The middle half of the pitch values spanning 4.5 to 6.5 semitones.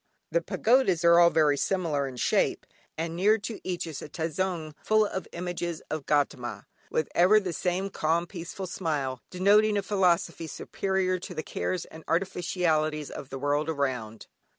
No: average, 3.5 semitones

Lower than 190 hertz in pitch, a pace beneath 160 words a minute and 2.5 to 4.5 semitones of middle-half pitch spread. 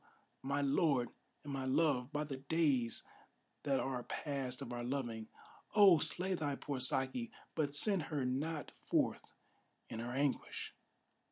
Yes: medium, 140 Hz; average, 145 wpm; average, 3.3 semitones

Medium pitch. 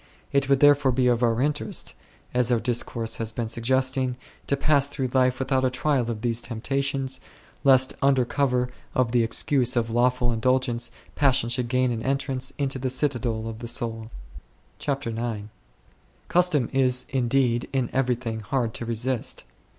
No: low, 125 Hz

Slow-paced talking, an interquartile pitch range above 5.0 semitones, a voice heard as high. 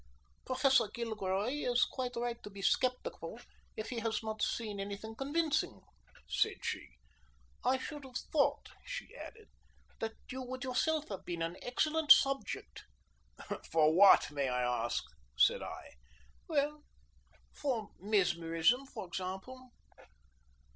Yes: slow, 130 wpm; wide, 5.5 semitones; high, 235 Hz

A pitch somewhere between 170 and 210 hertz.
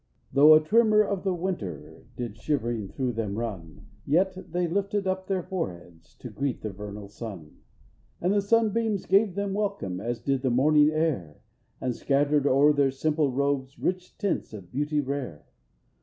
No: medium, 145 Hz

